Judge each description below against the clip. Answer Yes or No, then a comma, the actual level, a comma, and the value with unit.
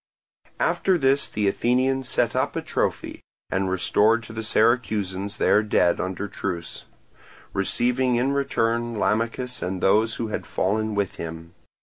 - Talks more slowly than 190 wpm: Yes, average, 140 wpm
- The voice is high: No, low, 110 Hz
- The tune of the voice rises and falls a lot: No, average, 3.8 semitones